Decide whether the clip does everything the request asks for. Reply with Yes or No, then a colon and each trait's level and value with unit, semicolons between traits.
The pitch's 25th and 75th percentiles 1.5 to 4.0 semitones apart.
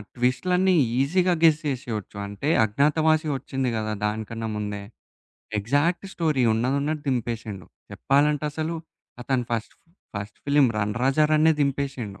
No: wide, 5.5 semitones